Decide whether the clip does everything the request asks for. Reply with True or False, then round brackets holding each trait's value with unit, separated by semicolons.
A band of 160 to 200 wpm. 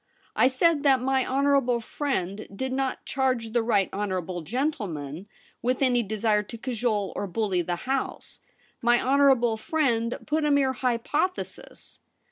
False (140 wpm)